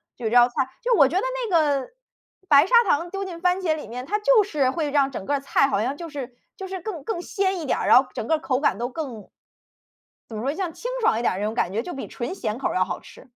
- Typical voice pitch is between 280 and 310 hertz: Yes, very high, 285 Hz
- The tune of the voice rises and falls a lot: Yes, wide, 6.7 semitones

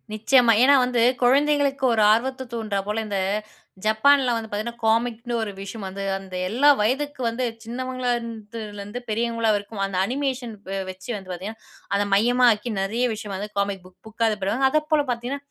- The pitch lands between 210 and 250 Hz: Yes, high, 230 Hz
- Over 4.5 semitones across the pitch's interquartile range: No, average, 3.6 semitones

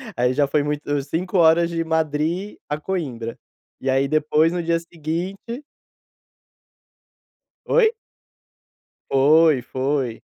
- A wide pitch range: No, average, 3.2 semitones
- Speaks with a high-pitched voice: No, medium, 155 Hz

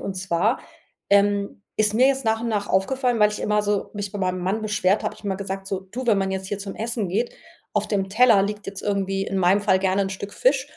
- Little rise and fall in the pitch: Yes, narrow, 2.0 semitones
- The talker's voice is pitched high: Yes, high, 200 Hz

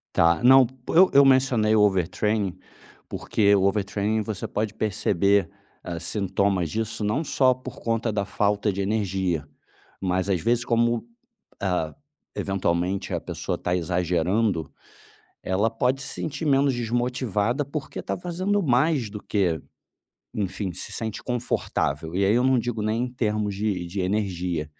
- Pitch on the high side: No, low, 105 Hz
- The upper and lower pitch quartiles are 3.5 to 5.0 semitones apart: Yes, average, 4.3 semitones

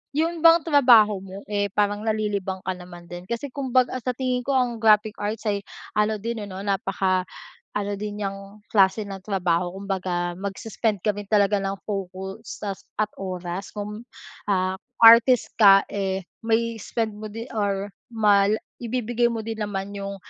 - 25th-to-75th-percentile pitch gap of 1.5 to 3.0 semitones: Yes, narrow, 2.6 semitones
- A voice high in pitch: Yes, high, 205 Hz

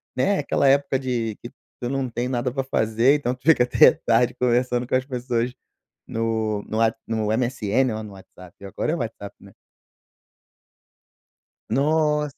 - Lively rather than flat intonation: No, average, 2.9 semitones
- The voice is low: Yes, low, 125 Hz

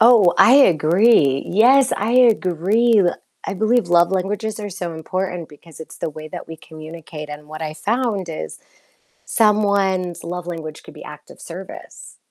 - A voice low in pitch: No, medium, 185 Hz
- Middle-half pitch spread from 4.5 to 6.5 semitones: Yes, average, 5.0 semitones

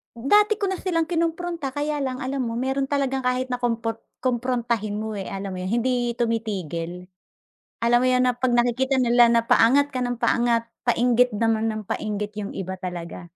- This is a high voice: Yes, high, 240 Hz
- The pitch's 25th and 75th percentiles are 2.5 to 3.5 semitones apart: Yes, average, 2.8 semitones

